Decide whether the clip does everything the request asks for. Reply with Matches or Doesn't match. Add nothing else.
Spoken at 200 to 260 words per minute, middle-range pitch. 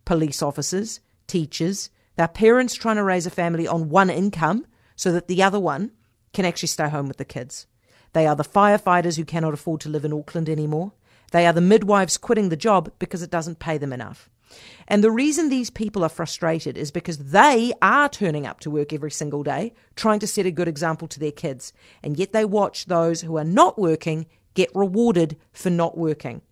Matches